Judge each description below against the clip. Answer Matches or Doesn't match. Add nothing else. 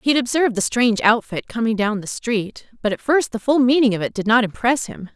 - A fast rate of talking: Matches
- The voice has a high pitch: Matches